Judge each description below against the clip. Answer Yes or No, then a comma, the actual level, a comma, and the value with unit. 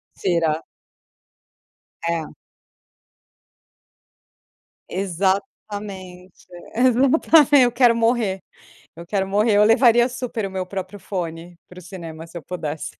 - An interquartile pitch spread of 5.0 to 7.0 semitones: Yes, wide, 5.4 semitones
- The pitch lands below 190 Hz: No, high, 195 Hz